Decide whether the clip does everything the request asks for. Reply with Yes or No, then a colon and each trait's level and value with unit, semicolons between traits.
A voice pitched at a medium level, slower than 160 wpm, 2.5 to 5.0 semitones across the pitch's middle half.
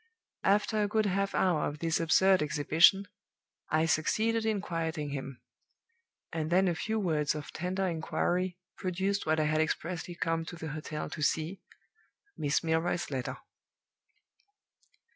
Yes: medium, 165 Hz; average, 140 wpm; average, 3.5 semitones